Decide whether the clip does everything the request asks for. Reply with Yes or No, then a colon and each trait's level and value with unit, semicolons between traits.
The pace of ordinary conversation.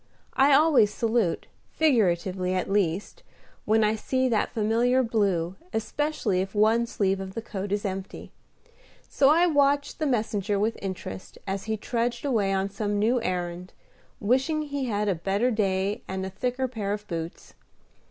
Yes: average, 160 wpm